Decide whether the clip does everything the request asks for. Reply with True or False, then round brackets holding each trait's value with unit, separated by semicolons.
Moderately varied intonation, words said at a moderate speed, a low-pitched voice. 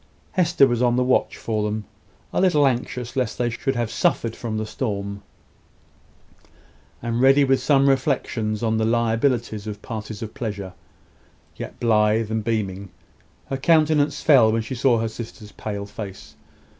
True (3.3 semitones; 160 wpm; 115 Hz)